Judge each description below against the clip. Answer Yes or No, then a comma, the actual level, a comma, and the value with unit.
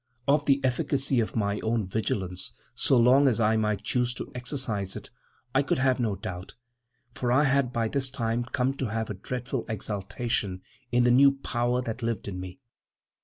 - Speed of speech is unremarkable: Yes, average, 185 wpm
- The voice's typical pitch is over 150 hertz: No, low, 120 Hz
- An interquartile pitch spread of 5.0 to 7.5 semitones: No, average, 3.4 semitones